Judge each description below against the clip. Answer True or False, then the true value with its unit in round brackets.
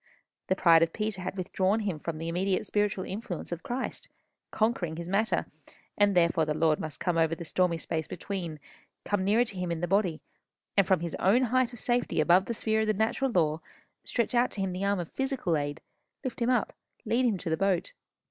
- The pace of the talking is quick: True (215 wpm)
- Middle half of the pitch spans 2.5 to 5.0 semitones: True (4.5 semitones)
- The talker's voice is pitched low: False (190 Hz)